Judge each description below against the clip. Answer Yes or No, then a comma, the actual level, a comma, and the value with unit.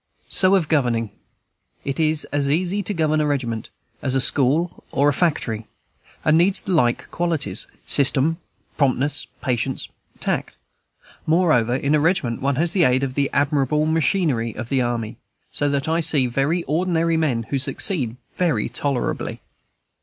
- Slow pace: No, average, 155 wpm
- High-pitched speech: No, medium, 145 Hz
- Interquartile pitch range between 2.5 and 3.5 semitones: No, average, 4.3 semitones